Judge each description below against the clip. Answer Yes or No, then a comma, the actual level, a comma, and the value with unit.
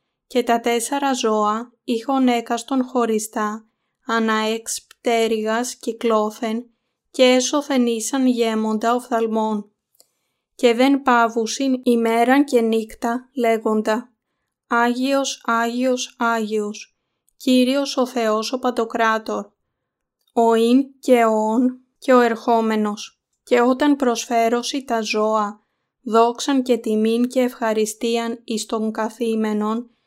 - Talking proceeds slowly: Yes, slow, 100 wpm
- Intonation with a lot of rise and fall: No, narrow, 2.3 semitones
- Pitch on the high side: Yes, high, 235 Hz